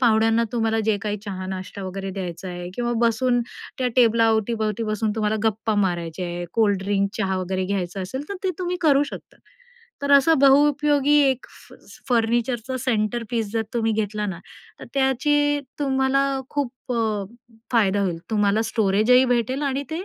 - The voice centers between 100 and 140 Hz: No, high, 225 Hz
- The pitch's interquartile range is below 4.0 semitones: No, average, 4.6 semitones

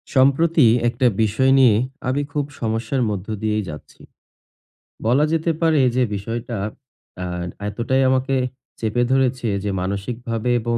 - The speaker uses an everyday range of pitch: Yes, average, 3.4 semitones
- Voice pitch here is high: No, low, 120 Hz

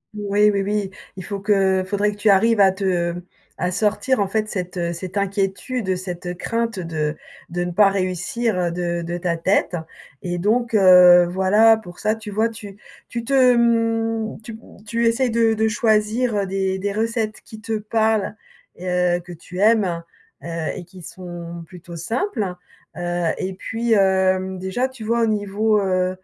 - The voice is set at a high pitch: Yes, high, 200 Hz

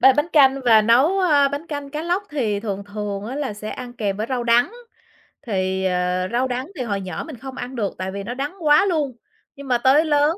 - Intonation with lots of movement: Yes, wide, 5.8 semitones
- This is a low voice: No, very high, 250 Hz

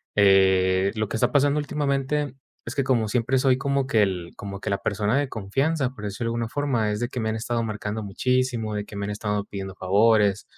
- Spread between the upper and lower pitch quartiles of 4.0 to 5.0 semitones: Yes, average, 4.3 semitones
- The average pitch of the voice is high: No, low, 110 Hz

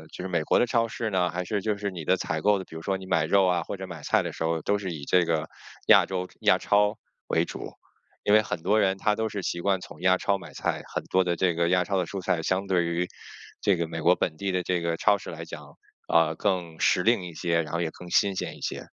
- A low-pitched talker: Yes, very low, 90 Hz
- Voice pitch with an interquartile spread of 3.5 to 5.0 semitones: No, average, 2.8 semitones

